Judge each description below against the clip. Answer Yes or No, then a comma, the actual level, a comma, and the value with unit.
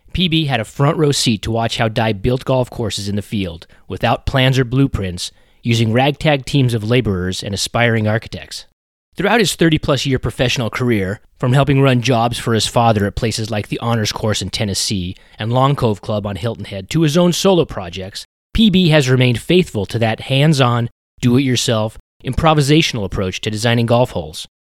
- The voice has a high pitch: No, low, 115 Hz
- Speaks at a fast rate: No, average, 190 wpm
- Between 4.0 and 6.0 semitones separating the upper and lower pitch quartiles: Yes, average, 4.6 semitones